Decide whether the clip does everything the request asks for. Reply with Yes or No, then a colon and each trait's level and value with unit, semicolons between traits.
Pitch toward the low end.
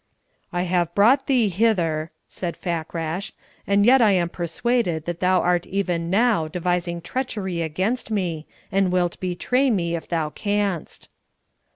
No: medium, 180 Hz